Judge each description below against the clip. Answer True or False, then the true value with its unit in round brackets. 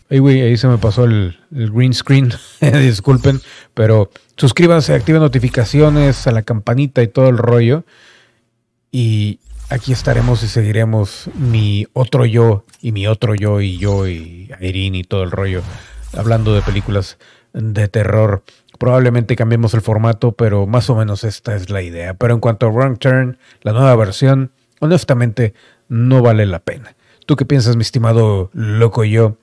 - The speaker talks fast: False (160 wpm)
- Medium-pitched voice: False (115 Hz)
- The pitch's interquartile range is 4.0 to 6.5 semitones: False (3.3 semitones)